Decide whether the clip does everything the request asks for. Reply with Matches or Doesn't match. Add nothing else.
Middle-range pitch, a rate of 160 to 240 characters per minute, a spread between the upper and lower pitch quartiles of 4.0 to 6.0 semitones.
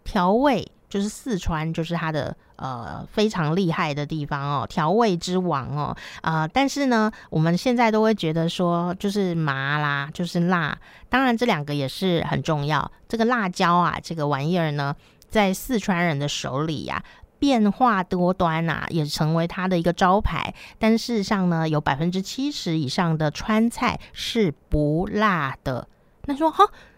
Doesn't match